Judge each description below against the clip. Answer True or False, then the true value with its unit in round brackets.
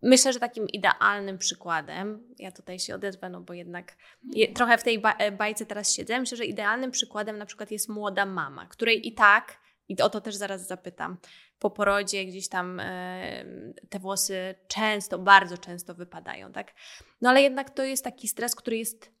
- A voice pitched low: False (210 Hz)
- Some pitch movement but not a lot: True (3.4 semitones)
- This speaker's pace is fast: True (180 wpm)